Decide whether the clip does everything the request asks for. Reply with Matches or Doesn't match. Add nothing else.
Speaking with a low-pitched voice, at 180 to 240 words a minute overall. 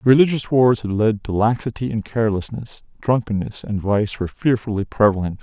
Doesn't match